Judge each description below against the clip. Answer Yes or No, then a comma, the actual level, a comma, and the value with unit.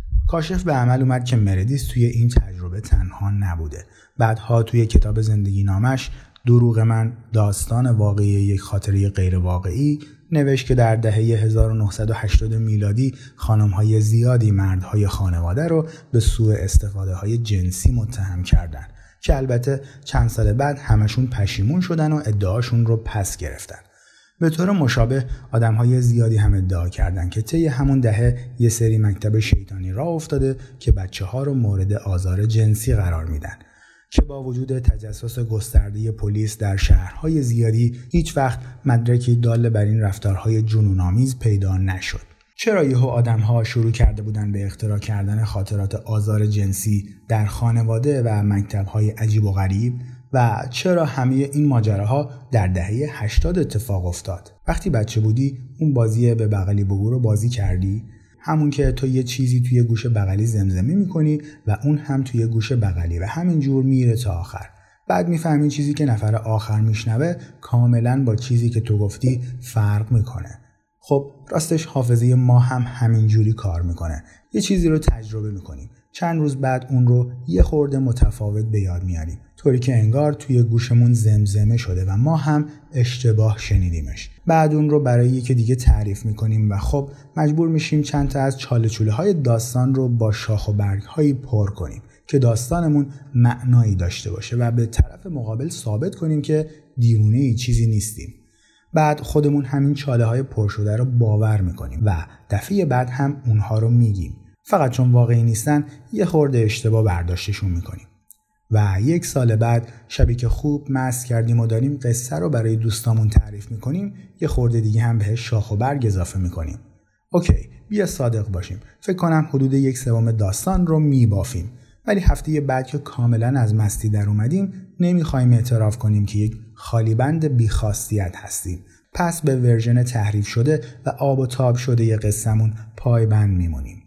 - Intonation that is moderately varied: Yes, average, 3.9 semitones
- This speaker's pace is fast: Yes, fast, 160 wpm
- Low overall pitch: Yes, low, 115 Hz